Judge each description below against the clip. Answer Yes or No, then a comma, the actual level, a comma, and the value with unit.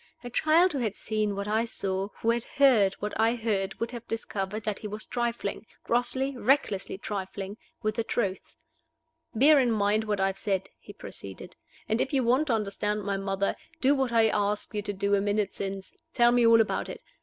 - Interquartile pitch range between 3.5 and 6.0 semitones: No, average, 3.1 semitones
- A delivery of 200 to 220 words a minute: Yes, fast, 205 wpm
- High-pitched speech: Yes, high, 215 Hz